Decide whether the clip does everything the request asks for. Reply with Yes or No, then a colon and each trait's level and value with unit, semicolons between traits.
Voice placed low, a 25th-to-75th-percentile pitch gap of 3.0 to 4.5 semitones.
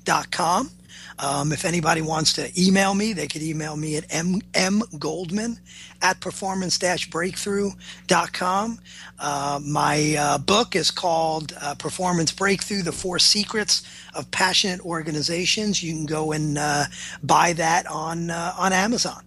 No: medium, 170 Hz; average, 3.6 semitones